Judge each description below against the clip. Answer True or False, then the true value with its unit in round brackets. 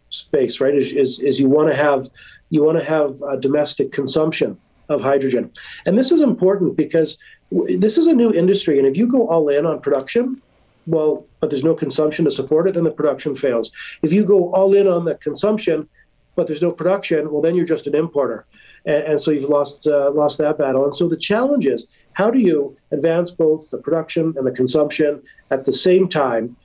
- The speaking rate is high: True (215 wpm)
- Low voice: False (155 Hz)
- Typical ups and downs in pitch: True (3.4 semitones)